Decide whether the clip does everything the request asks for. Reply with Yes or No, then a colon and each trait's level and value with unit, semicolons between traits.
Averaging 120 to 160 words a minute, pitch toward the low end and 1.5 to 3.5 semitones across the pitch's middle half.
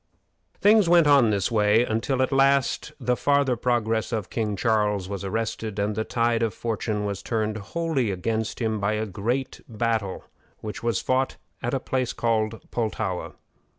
No: average, 170 wpm; low, 115 Hz; average, 3.0 semitones